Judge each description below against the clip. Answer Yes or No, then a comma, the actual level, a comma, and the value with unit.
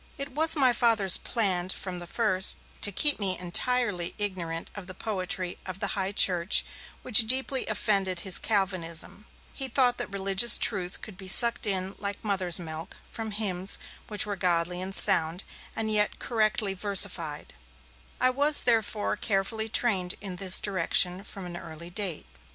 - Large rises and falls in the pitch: No, average, 3.3 semitones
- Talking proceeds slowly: No, average, 160 wpm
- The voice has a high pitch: Yes, high, 195 Hz